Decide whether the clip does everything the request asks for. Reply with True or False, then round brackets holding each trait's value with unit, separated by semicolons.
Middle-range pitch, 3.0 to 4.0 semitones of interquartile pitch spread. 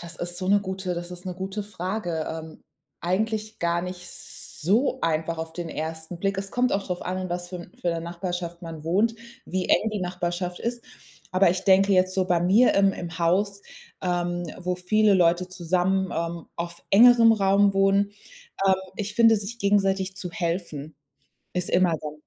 False (180 Hz; 2.4 semitones)